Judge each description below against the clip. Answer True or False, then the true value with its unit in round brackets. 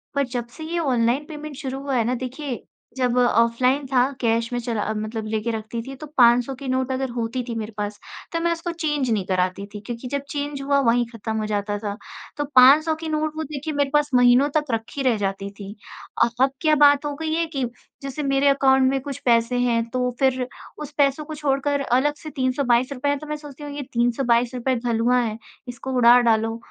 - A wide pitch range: False (3.5 semitones)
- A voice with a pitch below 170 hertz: False (255 Hz)